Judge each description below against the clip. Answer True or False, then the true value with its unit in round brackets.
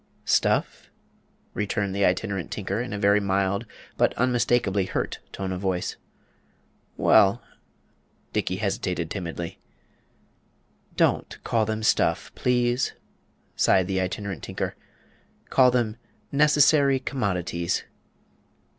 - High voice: False (100 Hz)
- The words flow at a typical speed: False (105 wpm)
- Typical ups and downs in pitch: True (4.4 semitones)